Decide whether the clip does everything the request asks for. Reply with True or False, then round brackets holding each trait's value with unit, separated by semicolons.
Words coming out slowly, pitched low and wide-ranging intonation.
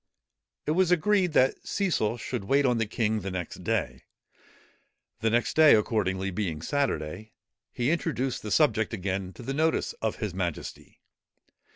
False (155 wpm; 115 Hz; 7.4 semitones)